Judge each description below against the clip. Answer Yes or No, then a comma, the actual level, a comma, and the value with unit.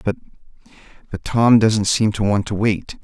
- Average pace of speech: Yes, average, 160 wpm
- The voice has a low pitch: Yes, low, 105 Hz